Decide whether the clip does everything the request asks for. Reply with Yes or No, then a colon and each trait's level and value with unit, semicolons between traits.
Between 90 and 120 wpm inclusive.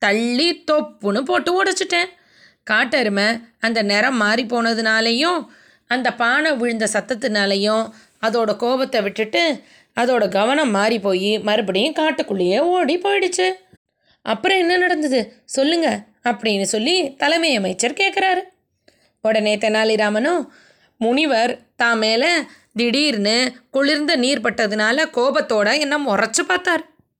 Yes: average, 100 wpm